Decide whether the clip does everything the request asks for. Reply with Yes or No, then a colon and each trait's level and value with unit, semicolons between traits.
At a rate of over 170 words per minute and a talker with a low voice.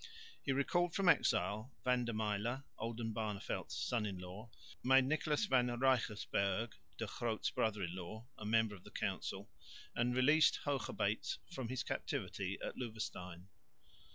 No: average, 140 wpm; low, 115 Hz